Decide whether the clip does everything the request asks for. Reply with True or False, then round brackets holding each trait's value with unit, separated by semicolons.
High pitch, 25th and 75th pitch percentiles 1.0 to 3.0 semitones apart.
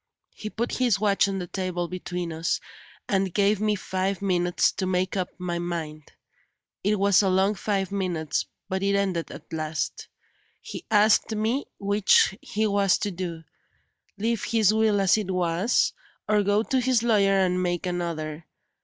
True (195 Hz; 2.7 semitones)